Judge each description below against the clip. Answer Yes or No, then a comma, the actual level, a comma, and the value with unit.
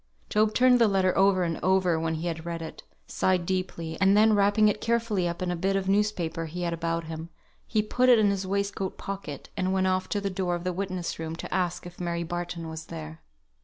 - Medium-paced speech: No, fast, 235 wpm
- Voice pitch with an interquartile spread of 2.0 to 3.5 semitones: Yes, average, 2.9 semitones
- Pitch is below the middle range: No, medium, 185 Hz